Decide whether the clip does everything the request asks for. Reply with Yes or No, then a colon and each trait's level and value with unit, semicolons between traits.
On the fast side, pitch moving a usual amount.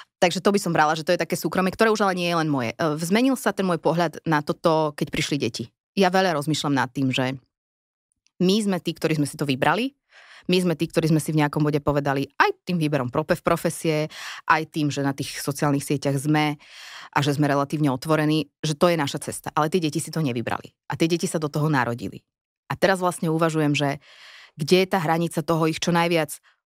Yes: fast, 225 wpm; average, 3.1 semitones